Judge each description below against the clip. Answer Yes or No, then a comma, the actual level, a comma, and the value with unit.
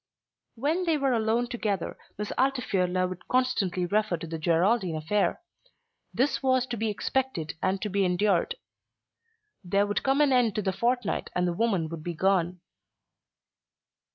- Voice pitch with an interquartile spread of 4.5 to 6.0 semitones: Yes, wide, 5.4 semitones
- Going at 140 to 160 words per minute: Yes, average, 155 wpm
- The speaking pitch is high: Yes, high, 205 Hz